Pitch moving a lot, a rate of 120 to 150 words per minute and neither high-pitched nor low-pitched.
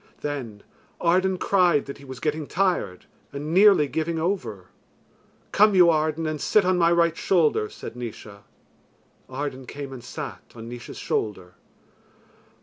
Yes: wide, 5.7 semitones; average, 145 wpm; medium, 150 Hz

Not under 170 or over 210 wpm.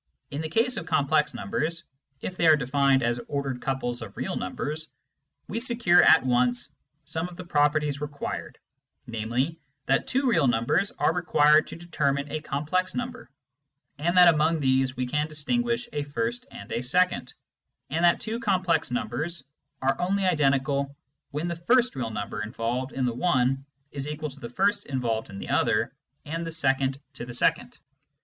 Yes: average, 175 wpm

